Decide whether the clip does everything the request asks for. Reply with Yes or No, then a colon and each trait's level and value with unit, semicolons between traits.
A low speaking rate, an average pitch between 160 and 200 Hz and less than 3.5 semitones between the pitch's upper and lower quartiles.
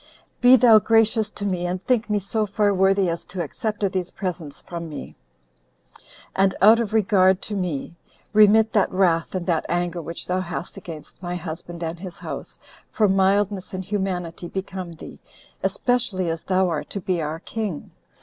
No: average, 180 wpm; medium, 185 Hz; average, 3.0 semitones